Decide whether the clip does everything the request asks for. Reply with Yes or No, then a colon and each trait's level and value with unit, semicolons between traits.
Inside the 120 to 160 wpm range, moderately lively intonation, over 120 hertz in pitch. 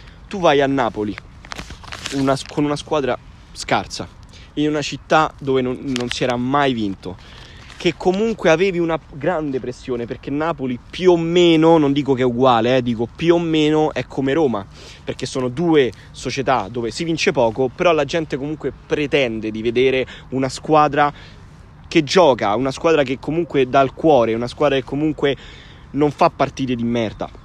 No: fast, 170 wpm; average, 3.9 semitones; medium, 140 Hz